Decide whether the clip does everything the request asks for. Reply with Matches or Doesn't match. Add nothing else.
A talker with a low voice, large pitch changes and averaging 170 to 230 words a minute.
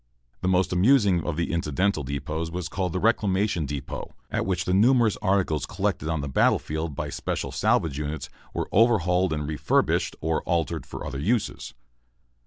Doesn't match